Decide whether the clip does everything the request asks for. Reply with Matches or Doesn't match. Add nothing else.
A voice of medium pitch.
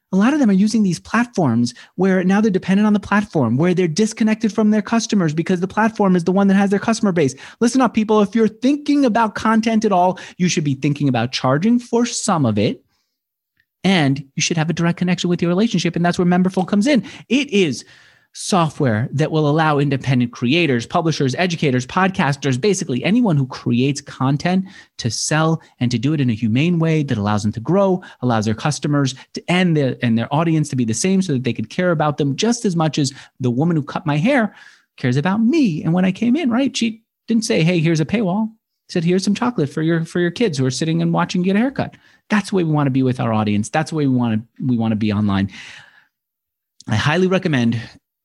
Matches